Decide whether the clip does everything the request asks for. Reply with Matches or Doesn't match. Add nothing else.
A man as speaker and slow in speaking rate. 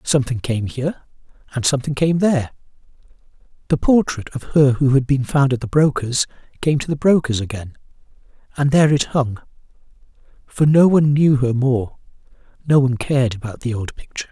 Doesn't match